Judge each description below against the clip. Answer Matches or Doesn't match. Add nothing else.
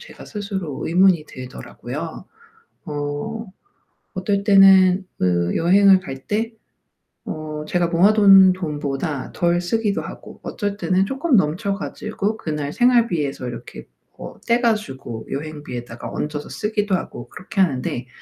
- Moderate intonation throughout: Doesn't match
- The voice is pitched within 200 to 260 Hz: Doesn't match